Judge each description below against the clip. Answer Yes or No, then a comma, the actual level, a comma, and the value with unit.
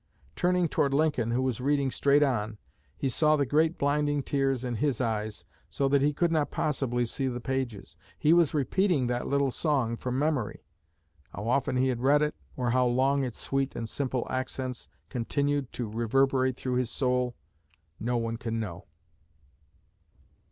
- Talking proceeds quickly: No, average, 170 wpm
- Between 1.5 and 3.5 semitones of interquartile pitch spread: Yes, average, 2.9 semitones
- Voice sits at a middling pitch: No, low, 130 Hz